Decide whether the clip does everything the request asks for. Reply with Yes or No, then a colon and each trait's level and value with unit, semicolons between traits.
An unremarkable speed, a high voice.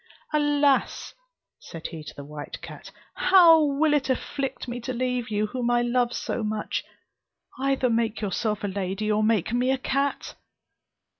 Yes: average, 160 wpm; high, 240 Hz